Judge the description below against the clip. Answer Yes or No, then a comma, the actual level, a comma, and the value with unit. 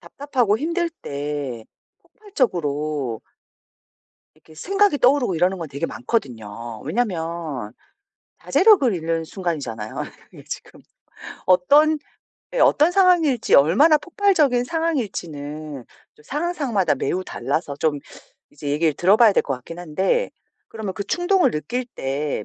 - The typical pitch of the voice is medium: Yes, medium, 180 Hz